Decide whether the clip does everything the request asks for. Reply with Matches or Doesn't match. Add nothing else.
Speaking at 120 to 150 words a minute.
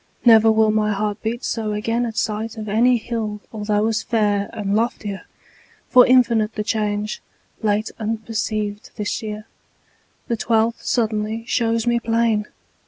Matches